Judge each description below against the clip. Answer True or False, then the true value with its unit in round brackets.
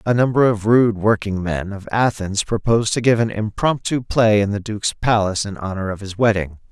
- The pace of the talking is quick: False (195 wpm)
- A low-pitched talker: True (105 Hz)